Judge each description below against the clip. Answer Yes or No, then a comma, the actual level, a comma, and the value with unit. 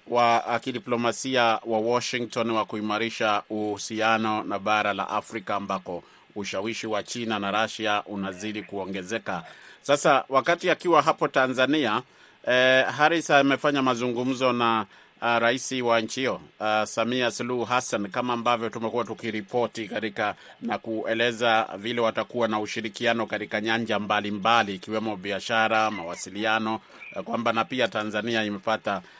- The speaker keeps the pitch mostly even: Yes, narrow, 2.1 semitones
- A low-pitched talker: Yes, low, 115 Hz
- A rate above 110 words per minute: Yes, average, 120 wpm